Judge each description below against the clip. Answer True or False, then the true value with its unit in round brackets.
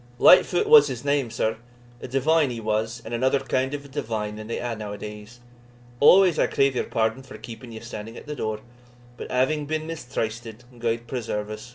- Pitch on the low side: True (120 Hz)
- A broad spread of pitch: False (4.0 semitones)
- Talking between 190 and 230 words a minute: True (200 wpm)